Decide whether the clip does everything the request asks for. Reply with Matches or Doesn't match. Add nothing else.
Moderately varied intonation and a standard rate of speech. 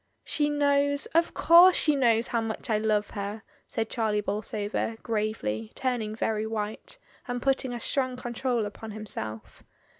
Matches